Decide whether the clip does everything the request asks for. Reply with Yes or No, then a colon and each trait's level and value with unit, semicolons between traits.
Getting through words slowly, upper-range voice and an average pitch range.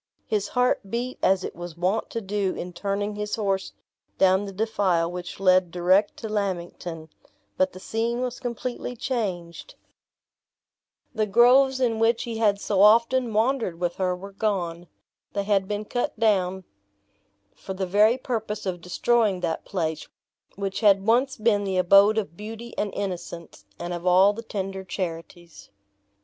No: average, 160 wpm; high, 200 Hz; average, 3.6 semitones